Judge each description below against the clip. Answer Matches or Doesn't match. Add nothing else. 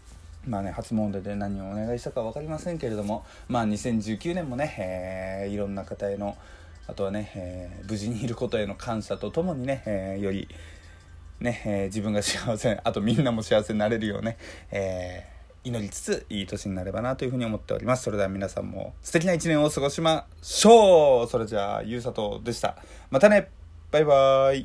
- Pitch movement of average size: Matches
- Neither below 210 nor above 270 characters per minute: Doesn't match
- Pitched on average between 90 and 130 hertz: Matches